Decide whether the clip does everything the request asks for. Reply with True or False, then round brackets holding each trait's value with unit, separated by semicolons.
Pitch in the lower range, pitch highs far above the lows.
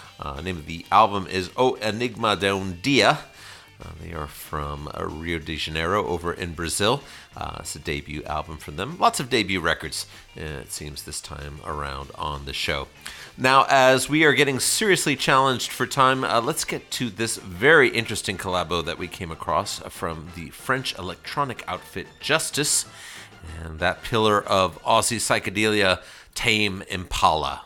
True (95 Hz; 6.1 semitones)